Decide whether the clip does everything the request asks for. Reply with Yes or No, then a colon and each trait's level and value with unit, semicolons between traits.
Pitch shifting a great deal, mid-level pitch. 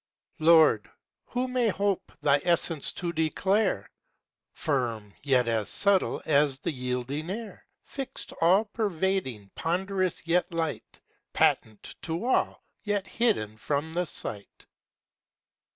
Yes: wide, 6.5 semitones; medium, 165 Hz